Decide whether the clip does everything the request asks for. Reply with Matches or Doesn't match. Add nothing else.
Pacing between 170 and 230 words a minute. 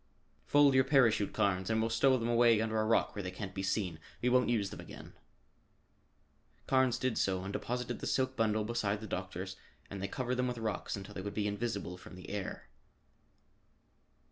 Matches